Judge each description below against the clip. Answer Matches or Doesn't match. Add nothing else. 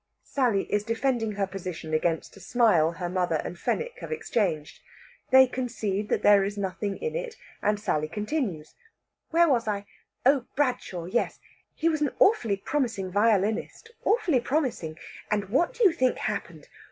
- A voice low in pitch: Doesn't match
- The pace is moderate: Matches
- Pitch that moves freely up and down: Matches